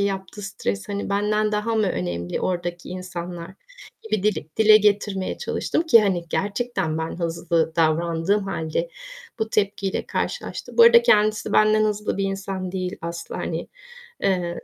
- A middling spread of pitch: Yes, average, 3.6 semitones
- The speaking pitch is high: Yes, high, 195 Hz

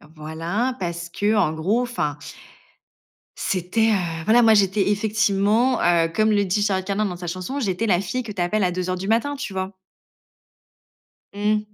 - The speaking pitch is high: Yes, high, 200 Hz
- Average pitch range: Yes, average, 3.5 semitones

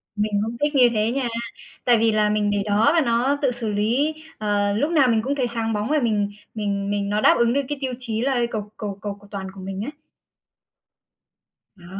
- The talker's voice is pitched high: Yes, high, 220 Hz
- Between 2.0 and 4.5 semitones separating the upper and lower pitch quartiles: Yes, average, 3.5 semitones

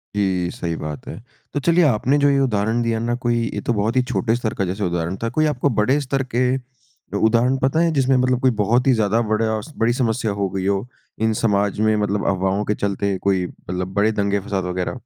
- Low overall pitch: Yes, low, 110 Hz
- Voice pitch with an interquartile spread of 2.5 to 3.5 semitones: No, average, 4.1 semitones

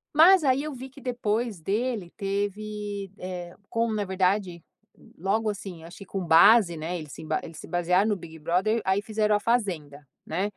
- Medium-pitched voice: No, high, 200 Hz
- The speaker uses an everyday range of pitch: Yes, average, 3.9 semitones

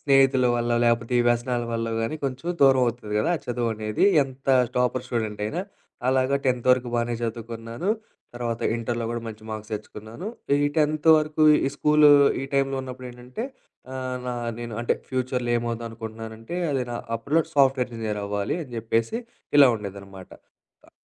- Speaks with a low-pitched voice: Yes, low, 120 Hz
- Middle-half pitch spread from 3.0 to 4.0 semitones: No, narrow, 2.6 semitones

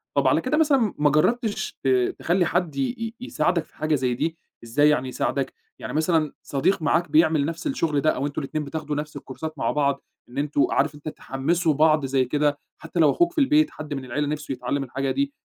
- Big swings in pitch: No, average, 3.6 semitones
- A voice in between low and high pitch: Yes, medium, 150 Hz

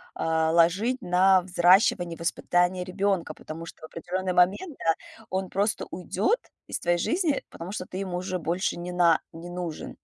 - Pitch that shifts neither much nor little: No, narrow, 2.0 semitones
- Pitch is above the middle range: No, medium, 180 Hz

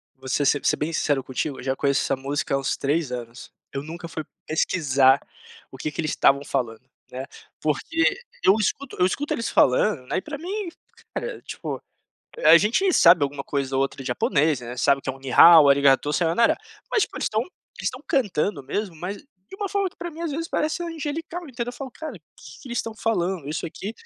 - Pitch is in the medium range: Yes, medium, 165 Hz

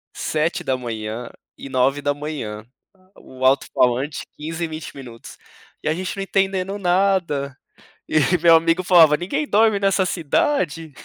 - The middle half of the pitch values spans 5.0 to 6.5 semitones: Yes, average, 5.3 semitones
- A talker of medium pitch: Yes, medium, 155 Hz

